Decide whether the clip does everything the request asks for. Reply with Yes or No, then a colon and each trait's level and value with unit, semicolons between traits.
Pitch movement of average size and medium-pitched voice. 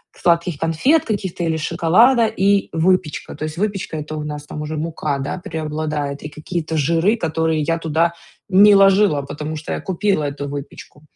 Yes: average, 3.6 semitones; medium, 160 Hz